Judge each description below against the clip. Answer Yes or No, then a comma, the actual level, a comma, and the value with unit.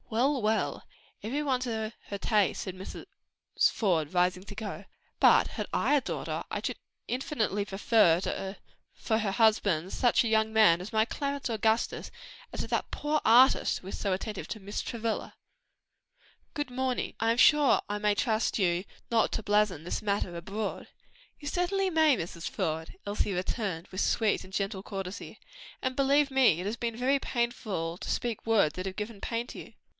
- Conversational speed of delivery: Yes, average, 185 wpm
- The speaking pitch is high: Yes, high, 220 Hz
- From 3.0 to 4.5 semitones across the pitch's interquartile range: Yes, average, 4.1 semitones